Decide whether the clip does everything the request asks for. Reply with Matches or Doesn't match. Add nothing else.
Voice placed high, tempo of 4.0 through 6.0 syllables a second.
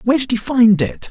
Matches